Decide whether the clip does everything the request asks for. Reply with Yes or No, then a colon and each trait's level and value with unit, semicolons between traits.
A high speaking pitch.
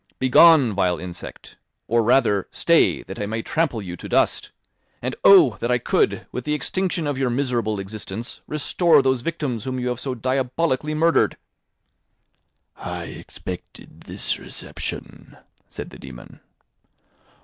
No: low, 125 Hz